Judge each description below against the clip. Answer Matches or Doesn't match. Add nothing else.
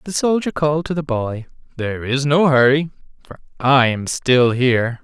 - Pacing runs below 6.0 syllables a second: Matches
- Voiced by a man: Matches